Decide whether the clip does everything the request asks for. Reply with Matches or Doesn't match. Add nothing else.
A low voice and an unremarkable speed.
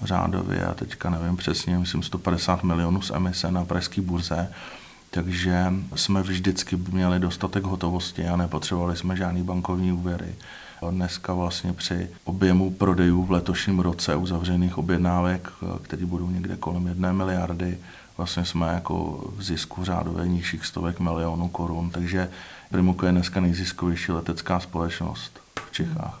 Matches